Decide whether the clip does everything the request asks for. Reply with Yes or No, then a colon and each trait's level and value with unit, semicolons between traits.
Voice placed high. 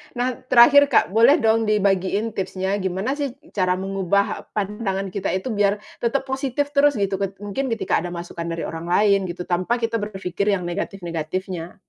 Yes: high, 200 Hz